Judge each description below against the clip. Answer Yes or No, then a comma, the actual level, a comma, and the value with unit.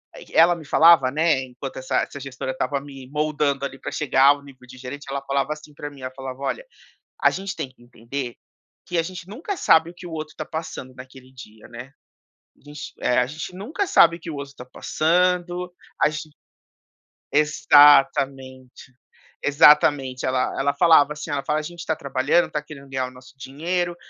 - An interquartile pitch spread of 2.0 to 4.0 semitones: Yes, average, 3.4 semitones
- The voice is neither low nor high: Yes, medium, 145 Hz